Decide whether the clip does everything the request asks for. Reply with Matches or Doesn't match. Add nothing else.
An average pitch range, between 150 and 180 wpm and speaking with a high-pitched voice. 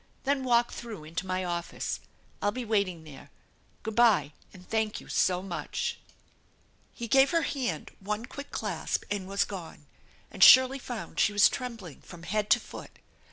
Matches